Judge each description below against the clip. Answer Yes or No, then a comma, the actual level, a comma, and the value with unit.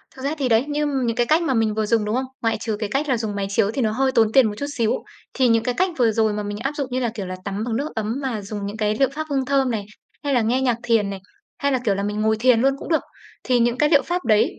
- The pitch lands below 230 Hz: No, high, 235 Hz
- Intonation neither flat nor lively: Yes, average, 3.9 semitones